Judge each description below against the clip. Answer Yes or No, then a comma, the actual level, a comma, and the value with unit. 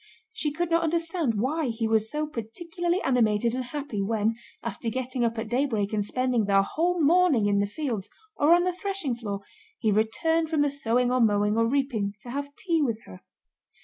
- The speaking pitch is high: Yes, very high, 250 Hz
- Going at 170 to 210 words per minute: Yes, average, 195 wpm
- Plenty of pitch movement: Yes, wide, 6.2 semitones